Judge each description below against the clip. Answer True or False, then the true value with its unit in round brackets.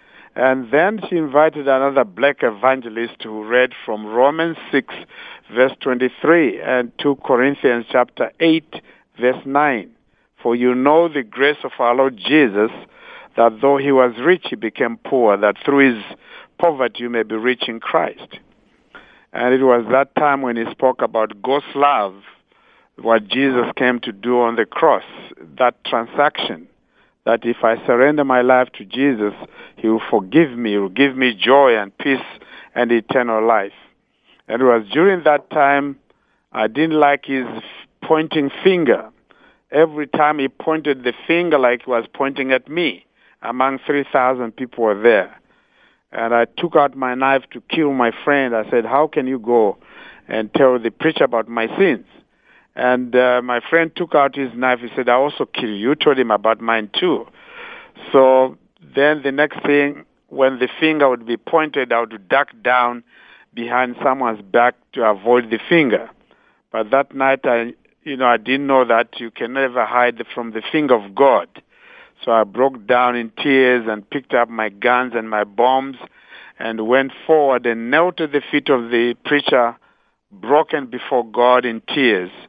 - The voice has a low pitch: True (130 Hz)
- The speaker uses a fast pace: False (170 wpm)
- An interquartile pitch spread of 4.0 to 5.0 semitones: False (3.1 semitones)